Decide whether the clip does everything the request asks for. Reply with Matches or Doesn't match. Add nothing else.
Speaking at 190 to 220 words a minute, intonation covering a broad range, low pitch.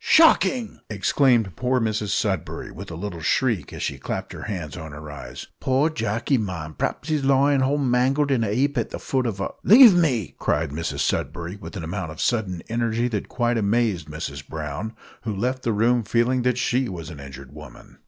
Matches